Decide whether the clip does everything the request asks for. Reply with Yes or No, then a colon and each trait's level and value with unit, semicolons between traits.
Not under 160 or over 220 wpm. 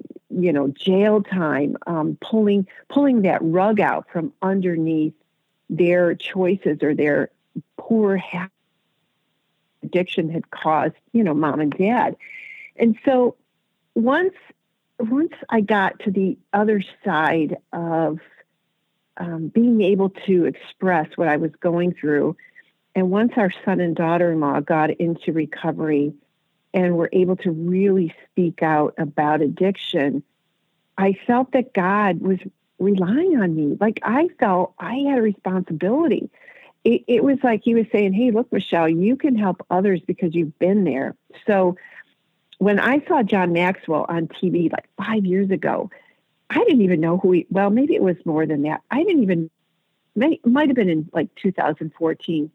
No: average, 150 wpm